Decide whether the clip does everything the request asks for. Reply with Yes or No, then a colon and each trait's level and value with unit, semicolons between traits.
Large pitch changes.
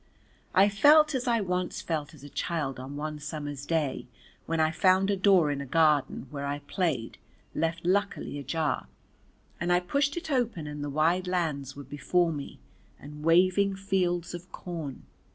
No: average, 4.2 semitones